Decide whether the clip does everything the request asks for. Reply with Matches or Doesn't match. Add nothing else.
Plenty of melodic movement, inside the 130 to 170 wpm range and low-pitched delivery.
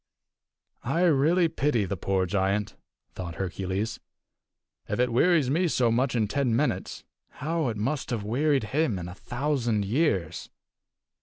Matches